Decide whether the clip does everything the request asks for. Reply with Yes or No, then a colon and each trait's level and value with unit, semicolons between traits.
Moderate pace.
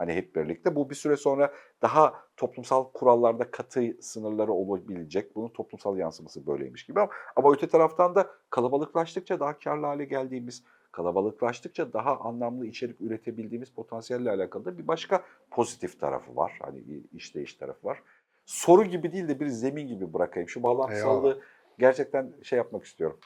No: fast, 150 wpm